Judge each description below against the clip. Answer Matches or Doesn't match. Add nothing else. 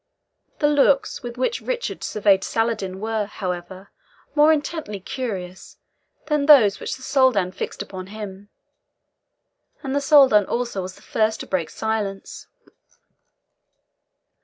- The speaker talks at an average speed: Doesn't match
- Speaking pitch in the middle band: Doesn't match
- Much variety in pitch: Matches